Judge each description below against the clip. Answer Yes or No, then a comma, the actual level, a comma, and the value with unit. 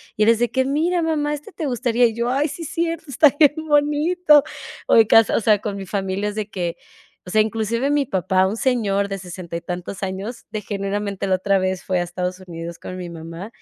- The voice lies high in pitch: Yes, high, 210 Hz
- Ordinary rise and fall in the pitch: No, wide, 6.5 semitones